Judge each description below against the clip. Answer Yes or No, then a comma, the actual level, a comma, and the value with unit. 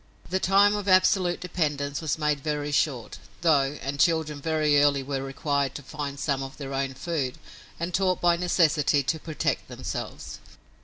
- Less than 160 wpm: No, average, 165 wpm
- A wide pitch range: No, average, 3.3 semitones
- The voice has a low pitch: No, medium, 150 Hz